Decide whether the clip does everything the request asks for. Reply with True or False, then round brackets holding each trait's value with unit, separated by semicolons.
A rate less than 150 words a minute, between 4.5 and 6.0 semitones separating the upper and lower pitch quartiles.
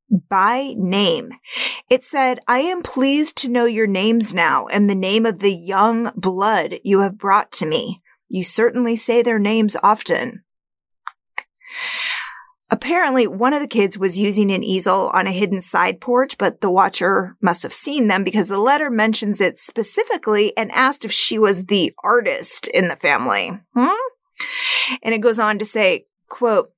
False (170 wpm; 4.8 semitones)